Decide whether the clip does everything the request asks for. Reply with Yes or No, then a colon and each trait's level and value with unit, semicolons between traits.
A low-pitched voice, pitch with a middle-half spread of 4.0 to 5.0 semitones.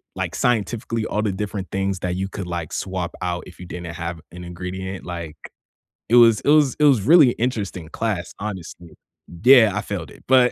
Yes: very low, 95 Hz; average, 4.6 semitones